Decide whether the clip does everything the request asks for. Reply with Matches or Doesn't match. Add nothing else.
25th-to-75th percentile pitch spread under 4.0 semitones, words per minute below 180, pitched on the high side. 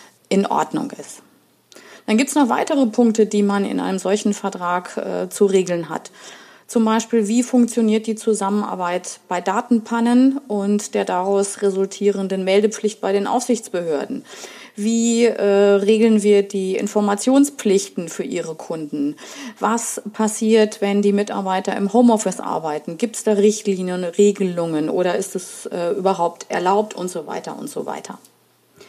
Matches